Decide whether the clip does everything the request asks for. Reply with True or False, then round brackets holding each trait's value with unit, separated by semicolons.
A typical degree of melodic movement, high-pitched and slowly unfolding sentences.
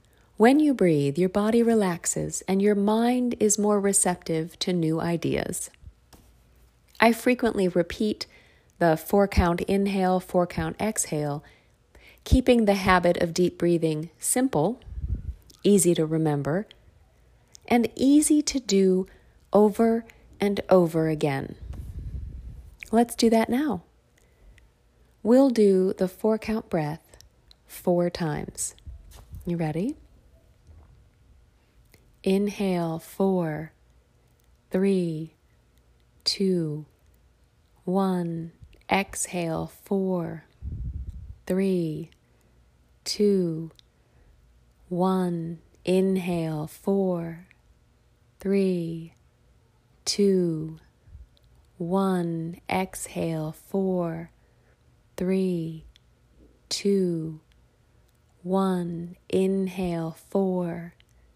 False (4.2 semitones; 175 Hz; 75 wpm)